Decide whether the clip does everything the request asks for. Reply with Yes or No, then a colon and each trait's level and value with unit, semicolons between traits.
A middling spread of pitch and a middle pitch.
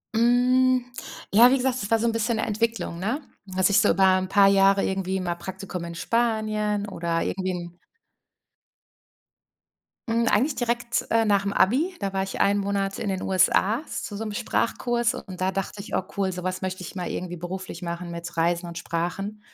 No: average, 3.6 semitones; high, 195 Hz